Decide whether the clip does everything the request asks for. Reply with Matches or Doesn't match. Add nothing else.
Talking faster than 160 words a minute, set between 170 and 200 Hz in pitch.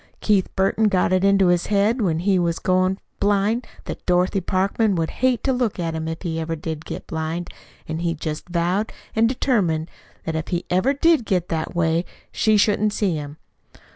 Matches